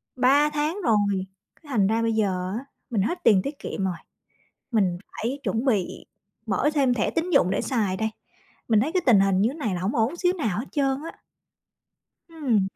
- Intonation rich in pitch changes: Yes, wide, 6.3 semitones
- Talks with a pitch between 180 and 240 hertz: Yes, high, 230 Hz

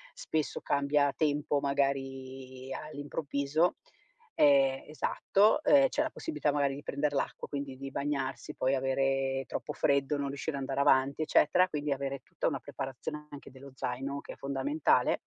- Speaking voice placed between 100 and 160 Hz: Yes, medium, 140 Hz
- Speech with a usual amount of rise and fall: No, narrow, 1.5 semitones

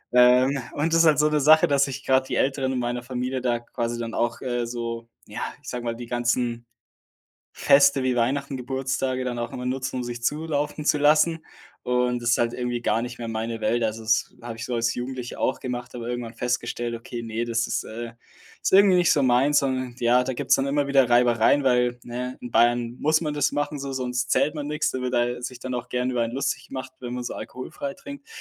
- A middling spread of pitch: No, narrow, 2.3 semitones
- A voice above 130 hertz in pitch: No, low, 125 Hz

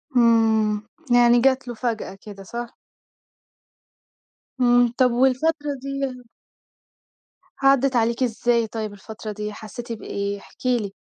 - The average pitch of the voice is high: Yes, high, 235 Hz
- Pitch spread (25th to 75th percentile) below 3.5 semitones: Yes, average, 2.7 semitones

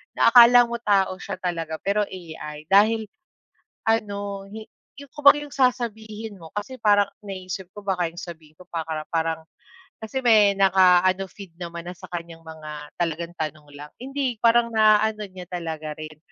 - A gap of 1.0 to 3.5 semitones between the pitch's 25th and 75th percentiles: No, average, 4.8 semitones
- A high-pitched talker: Yes, high, 195 Hz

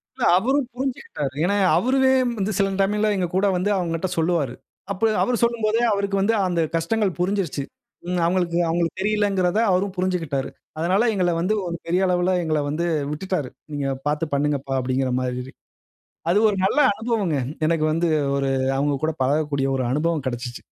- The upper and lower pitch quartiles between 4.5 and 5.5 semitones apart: Yes, average, 5.2 semitones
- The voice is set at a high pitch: No, medium, 175 Hz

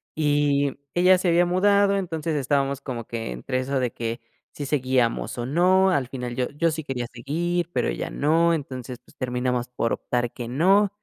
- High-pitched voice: No, medium, 140 Hz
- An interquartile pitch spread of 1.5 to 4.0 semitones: No, average, 5.3 semitones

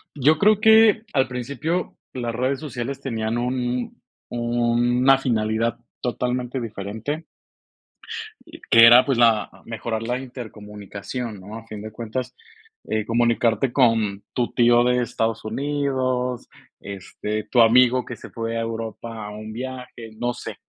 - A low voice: Yes, low, 120 Hz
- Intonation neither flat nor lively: No, narrow, 2.3 semitones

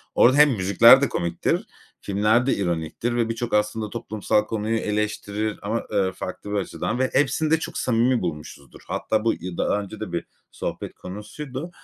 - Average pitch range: Yes, average, 3.1 semitones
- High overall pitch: No, low, 110 Hz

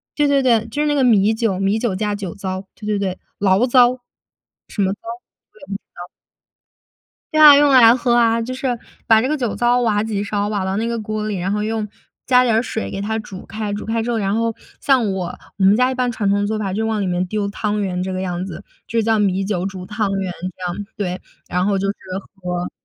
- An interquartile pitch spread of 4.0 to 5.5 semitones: No, average, 3.0 semitones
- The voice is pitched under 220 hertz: Yes, high, 210 Hz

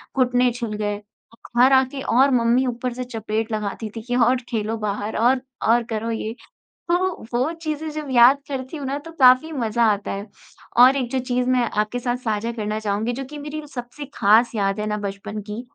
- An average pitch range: Yes, average, 3.3 semitones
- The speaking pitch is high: Yes, high, 240 Hz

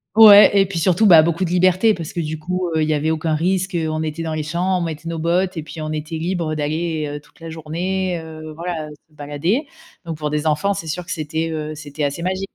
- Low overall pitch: No, medium, 165 Hz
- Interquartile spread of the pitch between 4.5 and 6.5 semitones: No, average, 2.7 semitones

